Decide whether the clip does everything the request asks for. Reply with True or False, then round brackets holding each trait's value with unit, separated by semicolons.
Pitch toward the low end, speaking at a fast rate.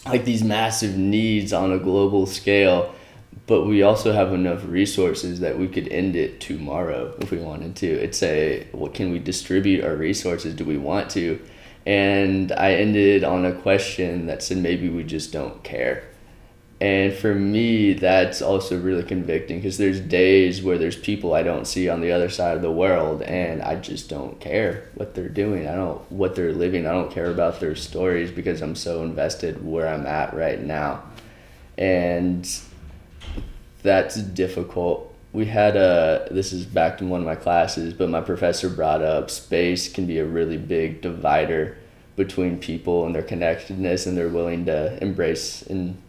False (90 Hz; 180 wpm)